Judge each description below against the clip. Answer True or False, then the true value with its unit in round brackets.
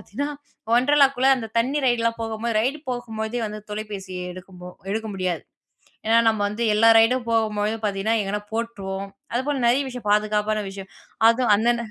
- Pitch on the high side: True (225 Hz)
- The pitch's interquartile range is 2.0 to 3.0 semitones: True (2.5 semitones)